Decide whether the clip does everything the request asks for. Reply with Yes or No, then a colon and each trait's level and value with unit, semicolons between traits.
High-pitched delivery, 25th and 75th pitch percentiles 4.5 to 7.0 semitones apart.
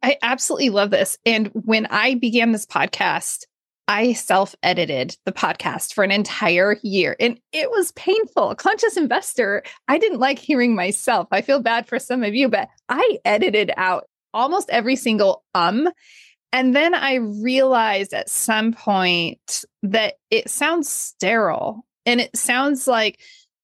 Yes: high, 240 Hz; average, 5.2 semitones